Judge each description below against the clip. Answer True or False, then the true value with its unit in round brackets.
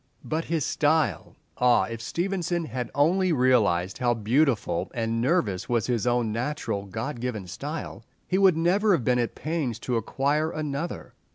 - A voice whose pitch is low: True (130 Hz)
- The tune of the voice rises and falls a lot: True (5.7 semitones)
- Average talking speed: True (160 wpm)